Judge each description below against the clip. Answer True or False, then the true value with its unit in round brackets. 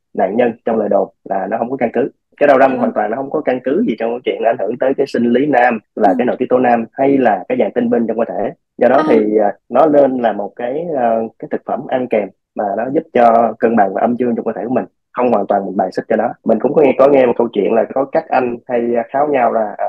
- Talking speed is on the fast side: True (300 wpm)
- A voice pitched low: True (120 Hz)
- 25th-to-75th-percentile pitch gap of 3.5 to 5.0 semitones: False (2.6 semitones)